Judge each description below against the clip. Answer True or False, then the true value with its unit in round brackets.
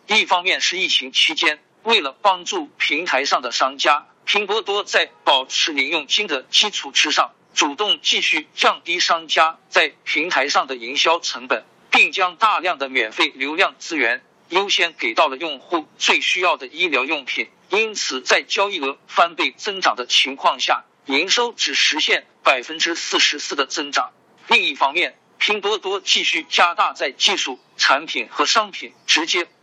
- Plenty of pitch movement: False (4.8 semitones)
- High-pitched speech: True (200 Hz)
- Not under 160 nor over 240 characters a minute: False (250 characters per minute)